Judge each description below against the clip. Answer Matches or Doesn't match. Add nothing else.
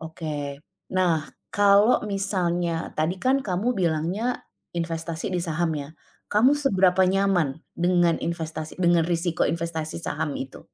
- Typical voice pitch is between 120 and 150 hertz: Doesn't match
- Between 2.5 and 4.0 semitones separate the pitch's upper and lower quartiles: Matches